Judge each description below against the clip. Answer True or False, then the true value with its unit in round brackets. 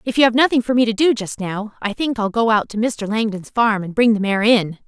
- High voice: True (220 Hz)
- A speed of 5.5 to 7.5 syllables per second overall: True (5.6 syllables/s)